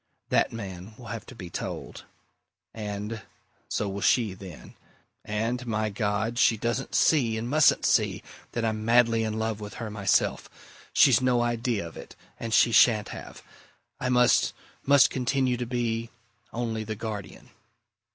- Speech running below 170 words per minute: Yes, average, 155 wpm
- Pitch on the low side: Yes, low, 115 Hz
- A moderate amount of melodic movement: No, narrow, 2.3 semitones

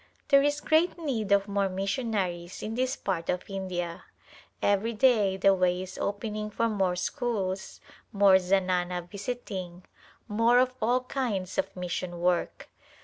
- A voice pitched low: No, high, 200 Hz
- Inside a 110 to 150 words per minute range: Yes, average, 145 wpm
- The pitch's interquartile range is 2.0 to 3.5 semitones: No, average, 4.0 semitones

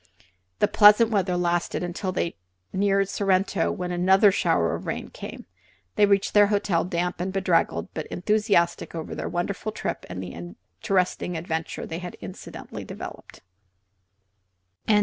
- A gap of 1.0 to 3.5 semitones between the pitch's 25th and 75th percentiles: Yes, average, 2.7 semitones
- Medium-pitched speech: Yes, medium, 180 Hz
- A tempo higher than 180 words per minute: No, average, 145 wpm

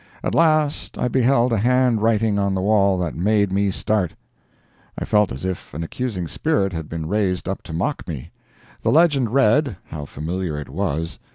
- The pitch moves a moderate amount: No, wide, 5.9 semitones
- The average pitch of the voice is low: Yes, low, 100 Hz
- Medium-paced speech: Yes, average, 185 wpm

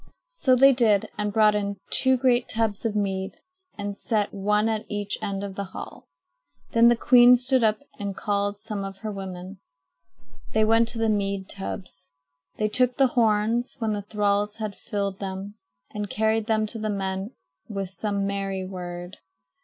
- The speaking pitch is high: Yes, high, 210 Hz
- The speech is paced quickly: No, average, 175 wpm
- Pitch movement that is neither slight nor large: No, narrow, 2.2 semitones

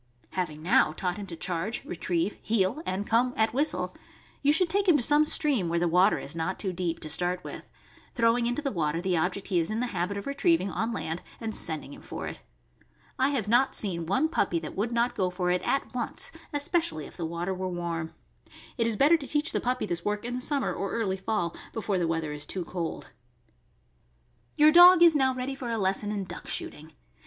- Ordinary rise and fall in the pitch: No, wide, 6.5 semitones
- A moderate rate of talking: No, fast, 220 wpm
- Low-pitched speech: No, high, 200 Hz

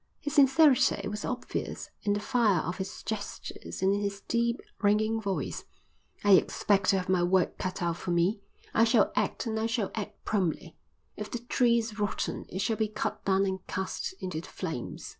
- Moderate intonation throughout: Yes, average, 3.0 semitones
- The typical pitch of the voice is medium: No, high, 205 Hz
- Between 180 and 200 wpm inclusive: Yes, average, 195 wpm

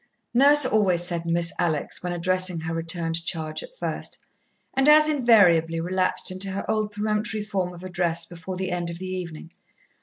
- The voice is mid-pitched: Yes, medium, 180 Hz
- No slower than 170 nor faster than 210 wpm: Yes, average, 175 wpm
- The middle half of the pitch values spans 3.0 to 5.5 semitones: Yes, average, 3.7 semitones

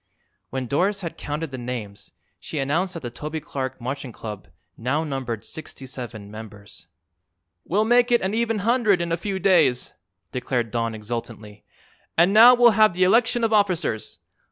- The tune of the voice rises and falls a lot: Yes, wide, 8.5 semitones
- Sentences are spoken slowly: No, average, 165 wpm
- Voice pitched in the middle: Yes, medium, 150 Hz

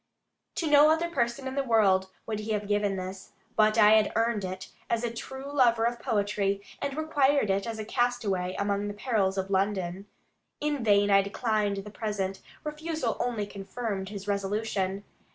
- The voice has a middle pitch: No, high, 210 Hz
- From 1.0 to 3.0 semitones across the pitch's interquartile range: No, average, 3.4 semitones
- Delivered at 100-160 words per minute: No, average, 175 wpm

